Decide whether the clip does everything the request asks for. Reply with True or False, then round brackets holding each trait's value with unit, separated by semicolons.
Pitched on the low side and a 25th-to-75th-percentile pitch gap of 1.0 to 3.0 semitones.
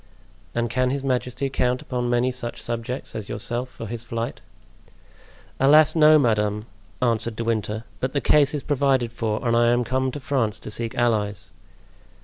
True (120 Hz; 2.4 semitones)